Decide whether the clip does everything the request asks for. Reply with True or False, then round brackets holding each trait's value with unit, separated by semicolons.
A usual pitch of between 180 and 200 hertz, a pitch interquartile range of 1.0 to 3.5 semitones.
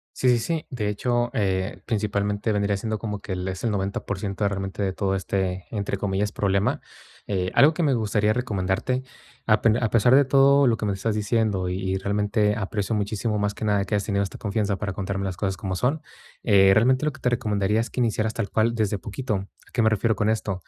False (105 Hz; 2.6 semitones)